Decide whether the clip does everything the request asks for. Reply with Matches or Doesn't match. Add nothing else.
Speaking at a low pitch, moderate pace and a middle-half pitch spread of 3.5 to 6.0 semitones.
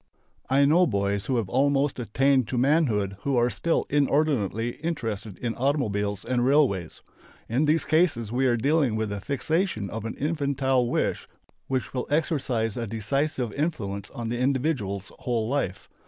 Matches